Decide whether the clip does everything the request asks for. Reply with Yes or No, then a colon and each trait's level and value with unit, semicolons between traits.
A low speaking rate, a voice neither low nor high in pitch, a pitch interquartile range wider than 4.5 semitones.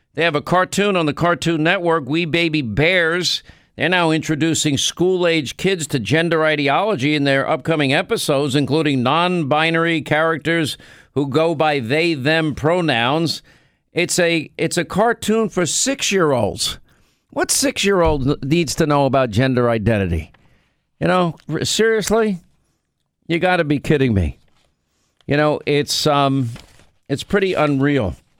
No: slow, 130 wpm; medium, 160 Hz; average, 3.4 semitones